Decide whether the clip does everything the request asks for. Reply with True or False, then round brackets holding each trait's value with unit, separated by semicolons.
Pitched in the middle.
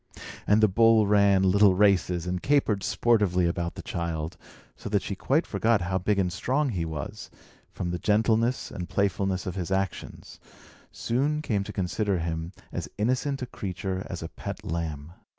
False (95 Hz)